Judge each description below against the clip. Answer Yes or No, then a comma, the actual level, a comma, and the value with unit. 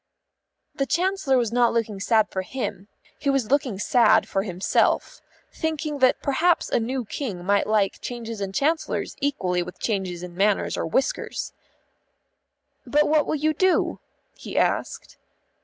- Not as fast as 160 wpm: Yes, average, 150 wpm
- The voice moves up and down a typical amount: No, wide, 6.2 semitones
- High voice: Yes, high, 240 Hz